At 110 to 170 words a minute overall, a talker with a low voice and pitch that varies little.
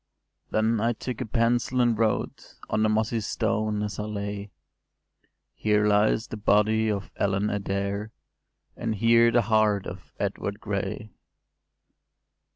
Yes: average, 140 wpm; low, 110 Hz; narrow, 1.6 semitones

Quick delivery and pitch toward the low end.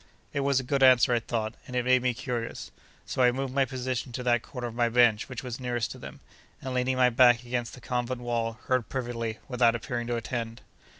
Yes: fast, 230 wpm; low, 125 Hz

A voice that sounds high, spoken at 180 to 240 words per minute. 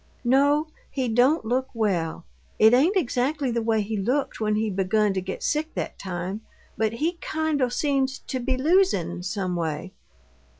No: high, 235 Hz; average, 170 wpm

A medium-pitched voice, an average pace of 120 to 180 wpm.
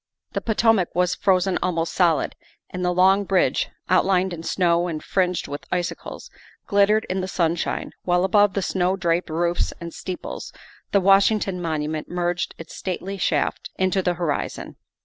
Yes: medium, 180 Hz; average, 160 wpm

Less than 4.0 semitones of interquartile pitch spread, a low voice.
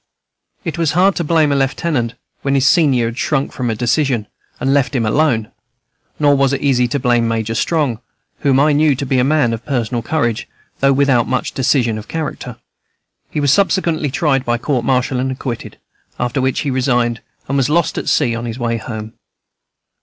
Yes: average, 3.4 semitones; low, 130 Hz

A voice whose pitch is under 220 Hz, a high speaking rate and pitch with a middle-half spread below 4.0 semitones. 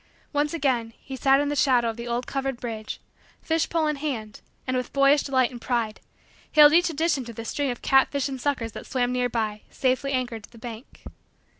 No: very high, 255 Hz; fast, 210 wpm; average, 3.2 semitones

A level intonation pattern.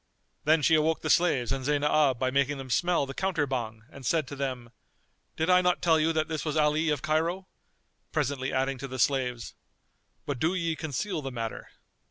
No: average, 3.4 semitones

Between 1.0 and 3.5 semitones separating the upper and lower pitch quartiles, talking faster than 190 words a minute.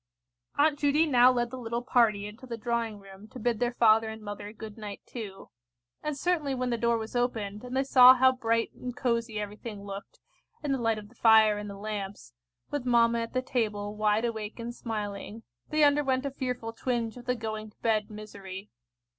Yes: average, 2.9 semitones; fast, 205 wpm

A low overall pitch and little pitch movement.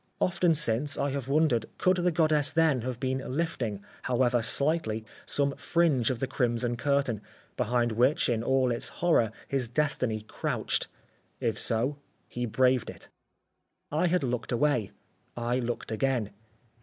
No: low, 130 Hz; average, 3.8 semitones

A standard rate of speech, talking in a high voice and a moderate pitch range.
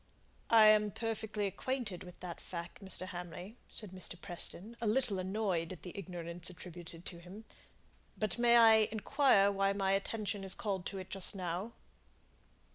Yes: average, 160 wpm; high, 195 Hz; average, 3.1 semitones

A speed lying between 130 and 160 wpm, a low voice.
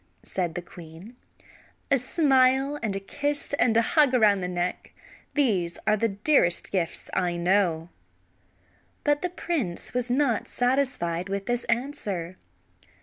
No: average, 140 wpm; high, 215 Hz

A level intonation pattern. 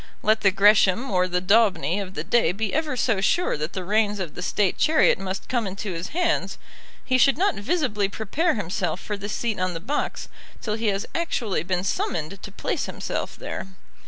No: average, 3.9 semitones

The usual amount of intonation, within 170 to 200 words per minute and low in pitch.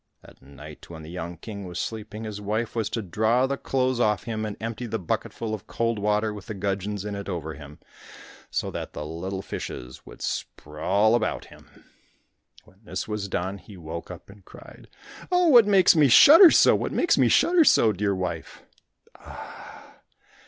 Yes: average, 4.1 semitones; average, 180 wpm; low, 105 Hz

